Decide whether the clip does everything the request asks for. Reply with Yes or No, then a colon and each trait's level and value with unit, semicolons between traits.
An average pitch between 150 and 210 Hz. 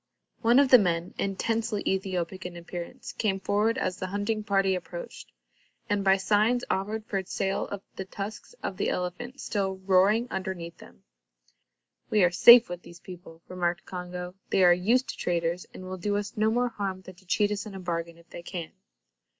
Yes: high, 190 Hz